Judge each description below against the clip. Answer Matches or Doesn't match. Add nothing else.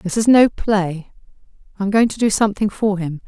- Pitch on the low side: Doesn't match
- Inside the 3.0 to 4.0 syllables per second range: Doesn't match